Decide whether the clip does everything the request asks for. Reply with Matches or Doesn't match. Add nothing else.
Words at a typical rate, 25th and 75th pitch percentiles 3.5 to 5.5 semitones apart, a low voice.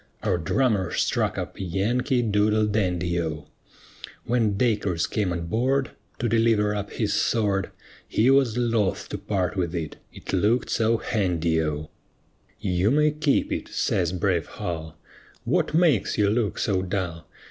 Matches